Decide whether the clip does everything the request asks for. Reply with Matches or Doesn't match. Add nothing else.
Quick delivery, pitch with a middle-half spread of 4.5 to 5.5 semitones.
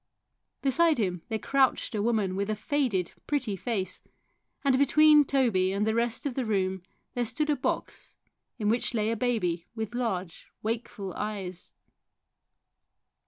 Doesn't match